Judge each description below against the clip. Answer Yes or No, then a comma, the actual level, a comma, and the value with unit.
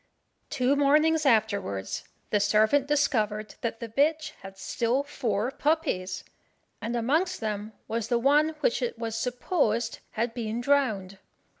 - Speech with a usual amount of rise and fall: Yes, average, 4.8 semitones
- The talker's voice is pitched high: Yes, high, 235 Hz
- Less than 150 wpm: Yes, slow, 135 wpm